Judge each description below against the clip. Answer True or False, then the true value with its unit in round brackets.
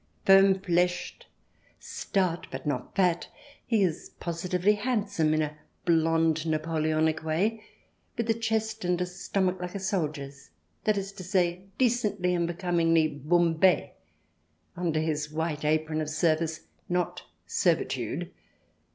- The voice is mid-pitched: True (175 Hz)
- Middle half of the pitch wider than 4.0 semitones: False (3.5 semitones)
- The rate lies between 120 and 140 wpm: True (135 wpm)